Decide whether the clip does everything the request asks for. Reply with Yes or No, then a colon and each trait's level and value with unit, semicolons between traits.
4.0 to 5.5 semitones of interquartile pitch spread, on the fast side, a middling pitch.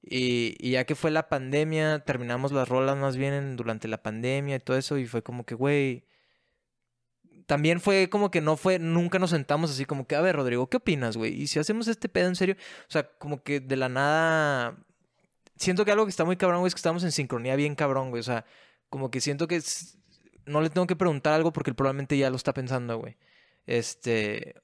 Yes: average, 4.4 semitones; fast, 225 wpm; medium, 145 Hz